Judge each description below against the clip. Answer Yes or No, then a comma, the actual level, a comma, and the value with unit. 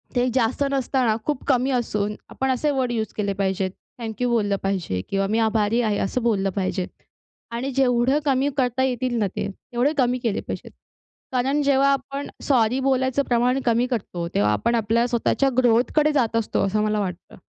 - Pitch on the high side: Yes, high, 240 Hz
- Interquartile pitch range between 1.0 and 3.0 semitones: No, average, 3.7 semitones